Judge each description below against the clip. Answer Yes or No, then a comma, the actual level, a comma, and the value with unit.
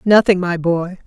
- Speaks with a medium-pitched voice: Yes, medium, 180 Hz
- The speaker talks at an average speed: Yes, average, 170 wpm